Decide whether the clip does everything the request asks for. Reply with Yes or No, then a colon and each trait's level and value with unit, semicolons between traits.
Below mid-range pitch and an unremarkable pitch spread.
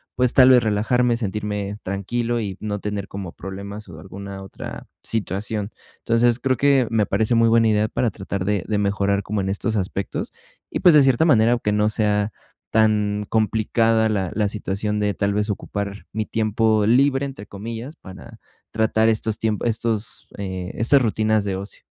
No: low, 105 Hz; narrow, 2.2 semitones